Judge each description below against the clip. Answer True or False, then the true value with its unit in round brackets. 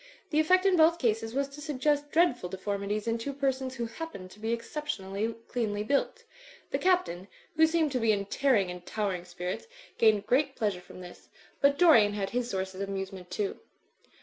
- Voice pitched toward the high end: True (230 Hz)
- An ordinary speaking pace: True (185 wpm)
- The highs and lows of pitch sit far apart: True (6.4 semitones)